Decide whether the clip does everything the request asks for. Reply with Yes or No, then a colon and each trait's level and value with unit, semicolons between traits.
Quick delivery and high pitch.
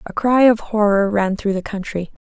Yes: fast, 210 wpm; high, 205 Hz